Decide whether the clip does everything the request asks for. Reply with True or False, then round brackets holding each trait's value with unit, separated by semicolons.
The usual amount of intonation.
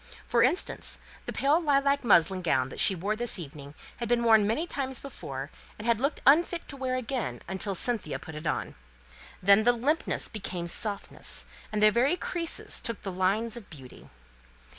False (6.2 semitones)